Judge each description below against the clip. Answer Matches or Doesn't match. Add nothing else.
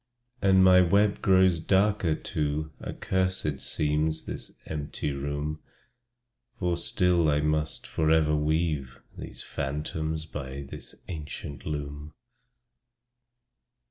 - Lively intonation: Doesn't match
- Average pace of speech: Doesn't match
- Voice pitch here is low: Matches